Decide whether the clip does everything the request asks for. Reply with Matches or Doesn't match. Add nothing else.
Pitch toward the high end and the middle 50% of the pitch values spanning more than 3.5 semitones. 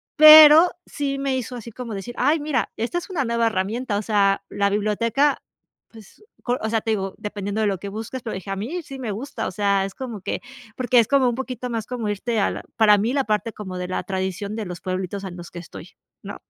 Matches